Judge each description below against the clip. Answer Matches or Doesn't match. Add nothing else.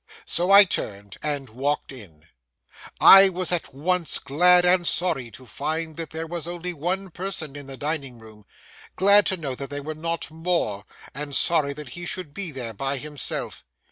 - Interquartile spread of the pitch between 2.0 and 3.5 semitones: Doesn't match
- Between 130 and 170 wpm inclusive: Doesn't match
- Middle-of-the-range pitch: Matches